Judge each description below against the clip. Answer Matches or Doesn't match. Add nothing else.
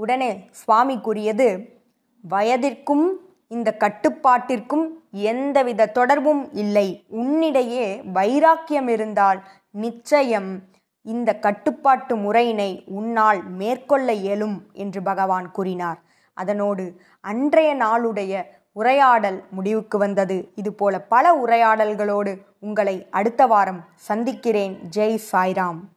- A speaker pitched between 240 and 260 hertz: Doesn't match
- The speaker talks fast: Doesn't match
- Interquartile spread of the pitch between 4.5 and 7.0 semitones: Doesn't match